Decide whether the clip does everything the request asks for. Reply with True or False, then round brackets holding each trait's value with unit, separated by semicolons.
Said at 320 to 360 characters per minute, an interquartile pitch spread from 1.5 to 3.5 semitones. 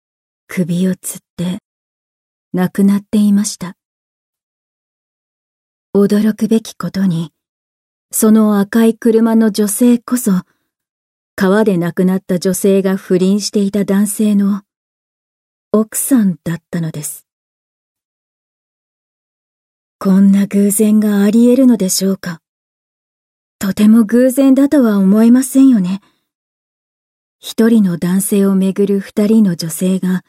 False (210 characters per minute; 2.8 semitones)